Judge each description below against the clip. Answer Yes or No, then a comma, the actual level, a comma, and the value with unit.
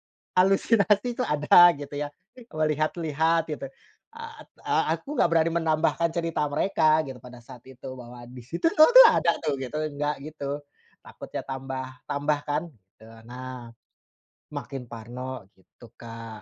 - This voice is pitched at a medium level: Yes, medium, 145 Hz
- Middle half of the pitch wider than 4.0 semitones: Yes, average, 4.6 semitones